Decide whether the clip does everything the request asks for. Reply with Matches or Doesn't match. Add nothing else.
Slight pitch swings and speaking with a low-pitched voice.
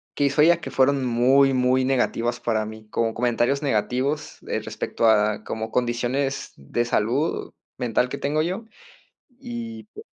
Doesn't match